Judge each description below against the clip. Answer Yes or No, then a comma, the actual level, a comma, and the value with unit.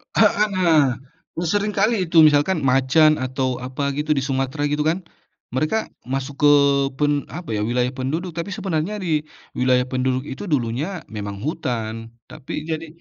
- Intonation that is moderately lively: Yes, average, 4.4 semitones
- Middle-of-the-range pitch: Yes, medium, 145 Hz